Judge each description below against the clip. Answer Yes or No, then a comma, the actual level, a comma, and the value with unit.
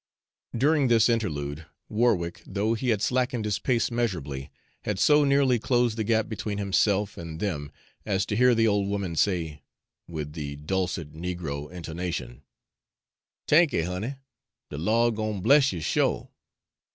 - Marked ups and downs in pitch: Yes, wide, 5.8 semitones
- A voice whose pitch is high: No, low, 100 Hz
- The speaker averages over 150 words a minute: No, average, 145 wpm